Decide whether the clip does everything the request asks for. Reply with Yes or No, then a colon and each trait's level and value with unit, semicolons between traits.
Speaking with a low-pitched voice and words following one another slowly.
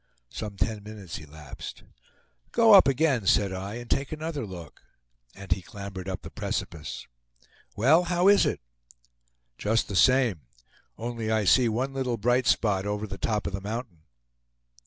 No: low, 110 Hz; average, 155 wpm